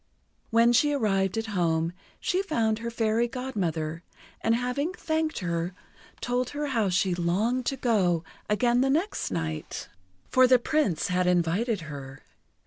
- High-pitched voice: Yes, high, 225 Hz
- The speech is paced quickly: No, average, 145 wpm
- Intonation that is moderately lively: No, wide, 6.3 semitones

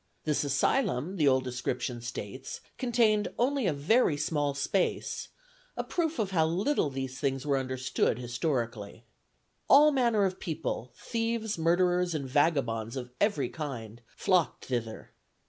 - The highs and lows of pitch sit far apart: Yes, wide, 7.6 semitones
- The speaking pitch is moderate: Yes, medium, 145 Hz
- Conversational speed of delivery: No, slow, 130 wpm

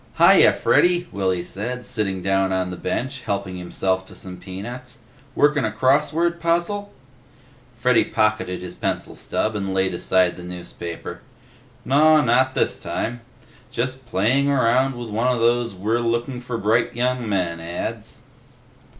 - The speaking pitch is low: Yes, low, 115 Hz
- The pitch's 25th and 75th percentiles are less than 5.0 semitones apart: No, average, 5.3 semitones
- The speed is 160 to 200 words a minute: No, average, 150 wpm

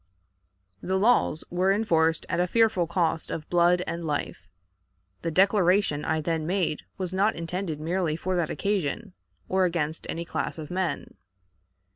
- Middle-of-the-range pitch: Yes, medium, 175 Hz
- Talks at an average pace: Yes, average, 150 wpm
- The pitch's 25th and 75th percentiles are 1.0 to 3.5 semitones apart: Yes, average, 2.8 semitones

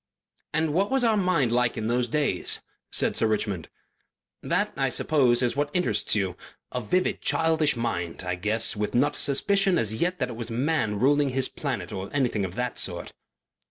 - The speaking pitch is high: No, low, 125 Hz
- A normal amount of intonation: No, wide, 6.1 semitones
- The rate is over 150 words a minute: Yes, average, 190 wpm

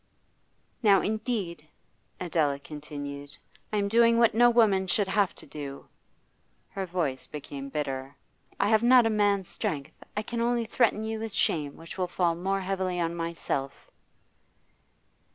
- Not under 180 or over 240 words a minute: No, average, 150 wpm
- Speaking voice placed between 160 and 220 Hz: Yes, medium, 185 Hz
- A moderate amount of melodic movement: No, wide, 6.4 semitones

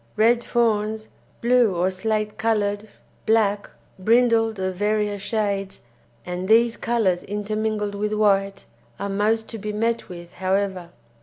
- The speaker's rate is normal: No, slow, 130 wpm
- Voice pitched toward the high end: Yes, high, 210 Hz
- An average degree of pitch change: No, narrow, 2.1 semitones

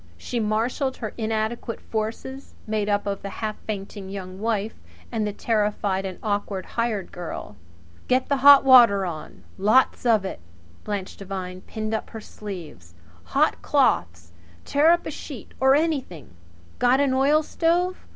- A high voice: Yes, high, 215 Hz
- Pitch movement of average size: Yes, average, 4.8 semitones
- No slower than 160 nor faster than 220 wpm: No, average, 150 wpm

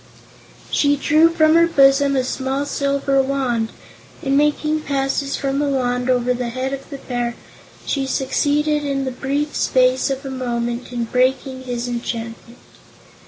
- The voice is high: Yes, very high, 270 Hz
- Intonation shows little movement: Yes, narrow, 2.2 semitones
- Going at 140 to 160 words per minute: Yes, average, 155 wpm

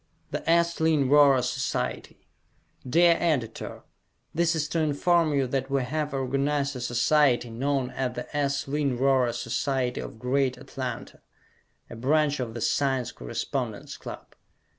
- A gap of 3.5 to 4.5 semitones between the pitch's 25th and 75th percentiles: No, average, 3.0 semitones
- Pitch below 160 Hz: Yes, low, 135 Hz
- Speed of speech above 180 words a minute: No, average, 140 wpm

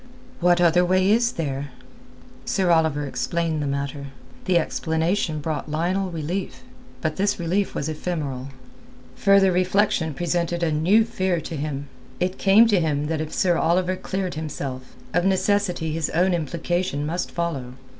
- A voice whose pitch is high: No, medium, 170 Hz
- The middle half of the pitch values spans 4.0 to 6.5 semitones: No, average, 3.3 semitones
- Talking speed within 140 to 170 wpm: Yes, average, 150 wpm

